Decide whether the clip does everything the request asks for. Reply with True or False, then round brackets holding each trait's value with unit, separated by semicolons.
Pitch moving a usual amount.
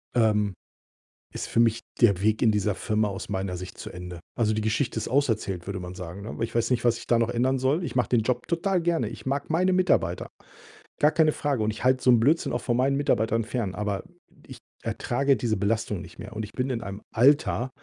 True (3.9 semitones)